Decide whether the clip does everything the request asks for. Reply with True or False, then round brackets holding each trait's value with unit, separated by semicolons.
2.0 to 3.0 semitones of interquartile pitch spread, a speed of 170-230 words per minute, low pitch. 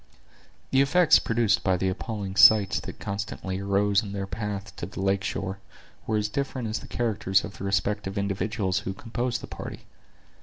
True (2.4 semitones; 180 wpm; 100 Hz)